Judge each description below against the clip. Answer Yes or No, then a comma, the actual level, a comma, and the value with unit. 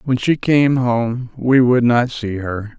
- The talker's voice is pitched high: No, low, 120 Hz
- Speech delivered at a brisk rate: No, average, 195 wpm